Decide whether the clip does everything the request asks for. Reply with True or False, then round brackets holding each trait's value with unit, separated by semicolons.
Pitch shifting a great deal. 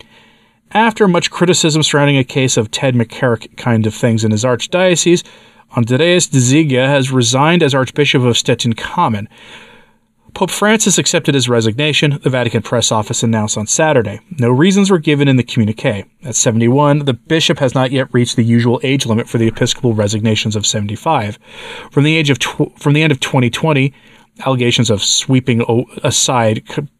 False (4.4 semitones)